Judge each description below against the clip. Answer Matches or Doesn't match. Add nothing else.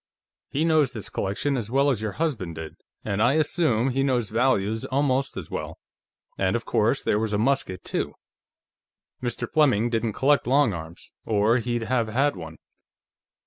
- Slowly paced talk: Doesn't match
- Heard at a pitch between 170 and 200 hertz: Doesn't match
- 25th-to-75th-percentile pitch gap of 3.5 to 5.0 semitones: Matches